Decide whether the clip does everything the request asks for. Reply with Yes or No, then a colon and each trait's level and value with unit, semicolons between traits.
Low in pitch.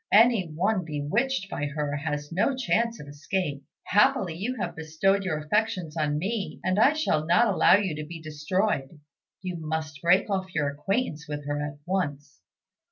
No: medium, 170 Hz